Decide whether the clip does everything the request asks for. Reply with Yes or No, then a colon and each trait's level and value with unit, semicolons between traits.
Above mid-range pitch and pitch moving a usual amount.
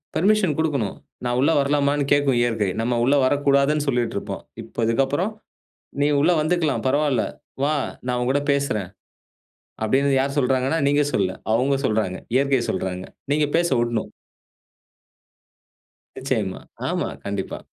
No: low, 135 Hz; average, 3.4 semitones